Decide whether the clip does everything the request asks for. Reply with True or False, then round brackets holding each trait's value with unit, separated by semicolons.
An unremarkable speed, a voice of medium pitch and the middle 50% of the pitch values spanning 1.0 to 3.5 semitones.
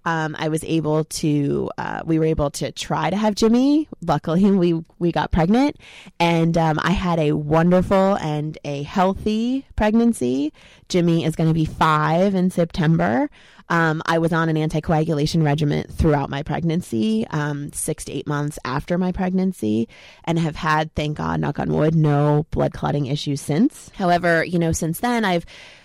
True (170 wpm; 160 Hz; 3.1 semitones)